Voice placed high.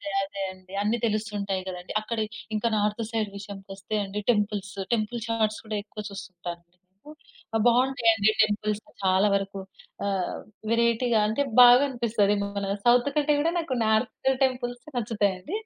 Yes: high, 215 Hz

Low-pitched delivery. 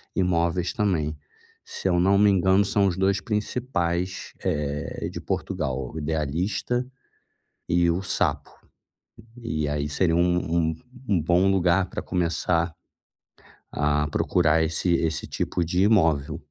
Yes: very low, 85 Hz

